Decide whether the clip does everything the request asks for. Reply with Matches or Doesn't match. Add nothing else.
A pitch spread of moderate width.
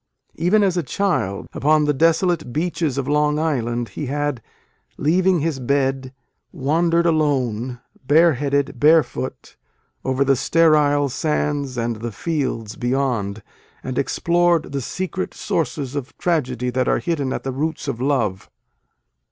Matches